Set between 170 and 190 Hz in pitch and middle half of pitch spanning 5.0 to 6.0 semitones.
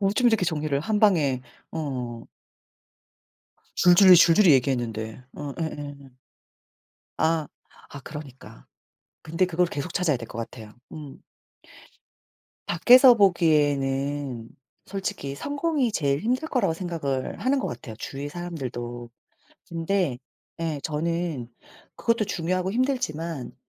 No: medium, 160 Hz; average, 5.3 semitones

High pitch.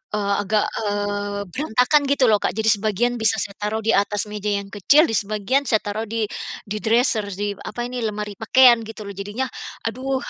Yes: high, 215 Hz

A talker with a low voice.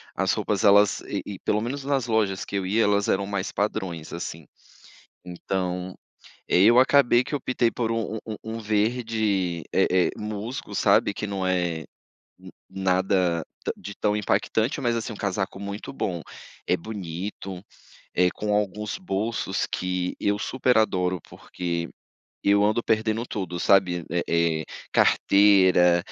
Yes: low, 100 Hz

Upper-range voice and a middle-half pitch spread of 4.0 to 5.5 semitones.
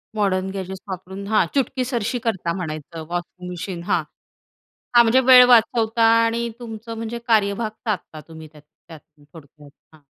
Yes: high, 200 Hz; average, 5.2 semitones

